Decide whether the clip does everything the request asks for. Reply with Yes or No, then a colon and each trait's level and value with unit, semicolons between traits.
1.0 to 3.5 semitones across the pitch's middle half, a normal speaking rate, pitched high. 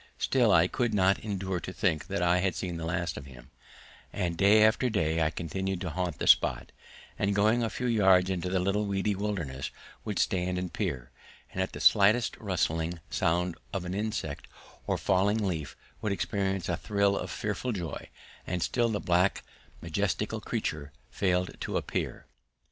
No: average, 3.0 semitones; average, 175 wpm; very low, 95 Hz